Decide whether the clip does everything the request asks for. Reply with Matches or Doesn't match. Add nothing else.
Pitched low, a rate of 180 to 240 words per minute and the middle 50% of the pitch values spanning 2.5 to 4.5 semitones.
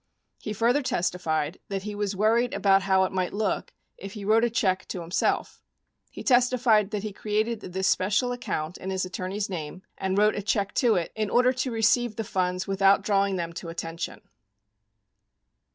Doesn't match